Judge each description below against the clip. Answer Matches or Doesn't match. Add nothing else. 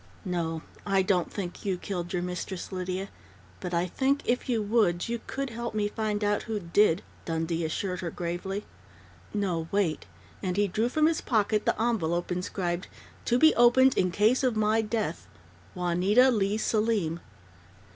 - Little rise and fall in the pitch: Doesn't match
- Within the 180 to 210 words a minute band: Doesn't match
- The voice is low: Doesn't match